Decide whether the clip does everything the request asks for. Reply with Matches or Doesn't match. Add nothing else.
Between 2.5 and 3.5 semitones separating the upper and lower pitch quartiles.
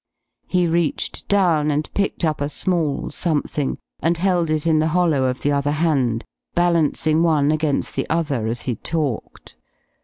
Matches